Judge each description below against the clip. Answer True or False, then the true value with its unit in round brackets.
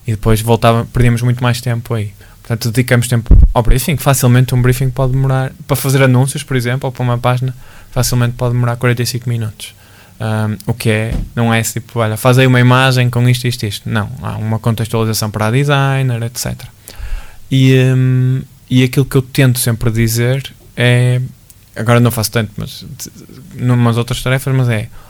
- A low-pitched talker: True (120 Hz)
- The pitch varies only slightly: True (2.2 semitones)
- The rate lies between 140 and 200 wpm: True (180 wpm)